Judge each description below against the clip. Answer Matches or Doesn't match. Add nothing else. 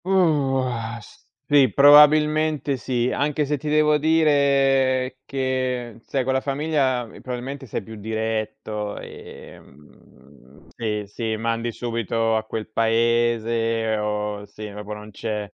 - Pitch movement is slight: Doesn't match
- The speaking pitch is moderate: Doesn't match